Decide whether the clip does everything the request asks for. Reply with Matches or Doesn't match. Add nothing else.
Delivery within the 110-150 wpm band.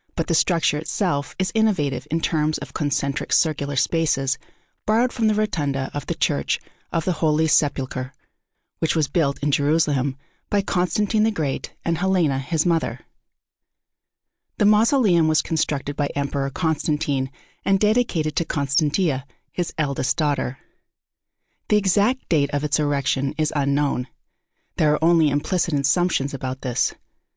Matches